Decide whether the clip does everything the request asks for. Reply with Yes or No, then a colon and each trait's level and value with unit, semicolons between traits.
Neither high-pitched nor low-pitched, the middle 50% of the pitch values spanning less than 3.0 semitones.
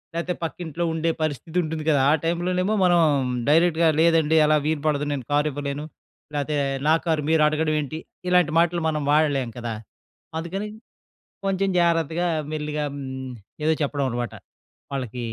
Yes: medium, 155 Hz; narrow, 2.6 semitones